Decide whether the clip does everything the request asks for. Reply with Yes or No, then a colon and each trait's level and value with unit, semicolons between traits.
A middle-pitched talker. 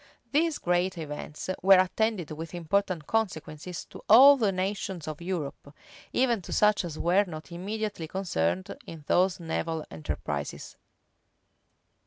Yes: medium, 180 Hz